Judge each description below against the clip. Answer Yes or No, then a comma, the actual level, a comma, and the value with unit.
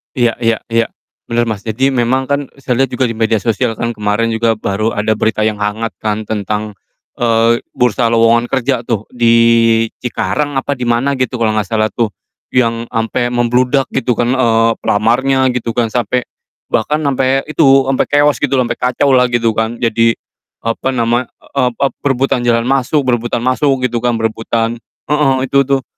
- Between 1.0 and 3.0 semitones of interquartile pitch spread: Yes, narrow, 2.4 semitones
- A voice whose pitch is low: Yes, low, 120 Hz